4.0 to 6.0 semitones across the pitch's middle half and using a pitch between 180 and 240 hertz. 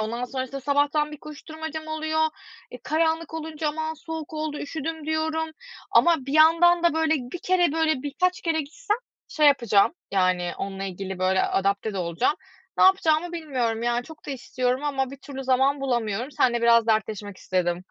No: average, 5.1 semitones; very high, 285 Hz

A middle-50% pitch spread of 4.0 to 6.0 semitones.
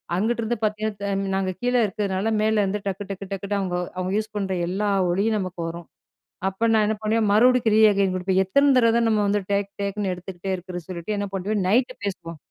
No: narrow, 2.4 semitones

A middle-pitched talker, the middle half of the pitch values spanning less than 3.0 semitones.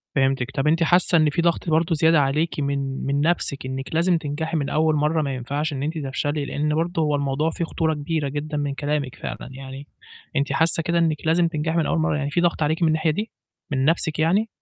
Yes: medium, 150 Hz; narrow, 2.6 semitones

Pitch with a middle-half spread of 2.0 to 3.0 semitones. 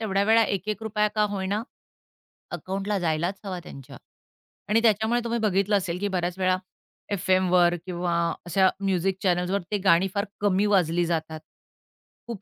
Yes: average, 2.7 semitones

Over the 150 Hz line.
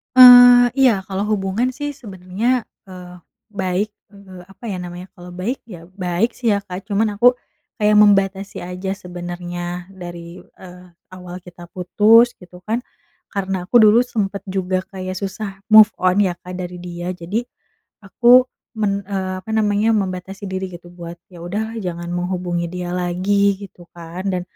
Yes: high, 190 Hz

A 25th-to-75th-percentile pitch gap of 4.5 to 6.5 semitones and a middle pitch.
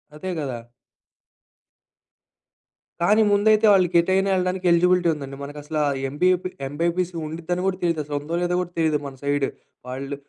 No: average, 3.8 semitones; medium, 170 Hz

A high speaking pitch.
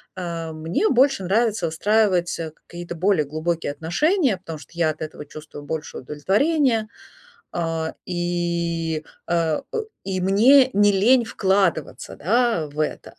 No: medium, 175 Hz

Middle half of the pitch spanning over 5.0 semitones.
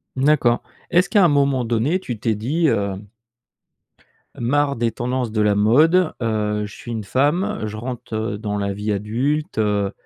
Yes: wide, 5.4 semitones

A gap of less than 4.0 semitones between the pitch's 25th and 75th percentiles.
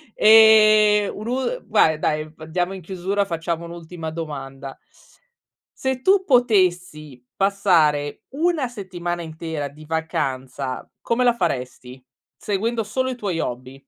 No: wide, 5.8 semitones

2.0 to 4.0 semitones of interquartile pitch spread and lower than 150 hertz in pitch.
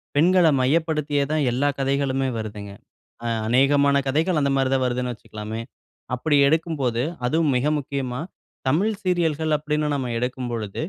Yes: average, 3.6 semitones; medium, 140 Hz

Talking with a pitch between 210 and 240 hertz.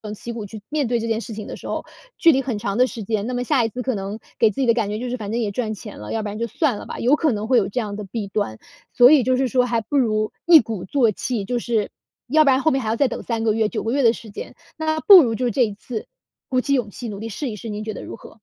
Yes: high, 230 Hz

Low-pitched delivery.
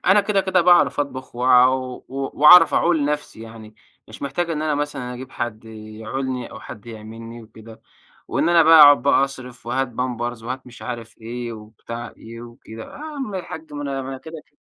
Yes: low, 130 Hz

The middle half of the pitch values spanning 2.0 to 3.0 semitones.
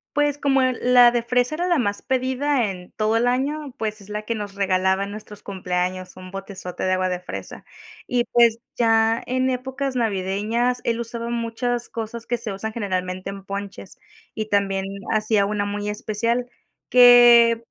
No: average, 3.6 semitones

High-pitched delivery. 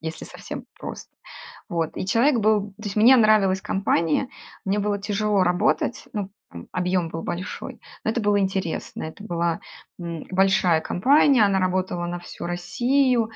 Yes: high, 195 Hz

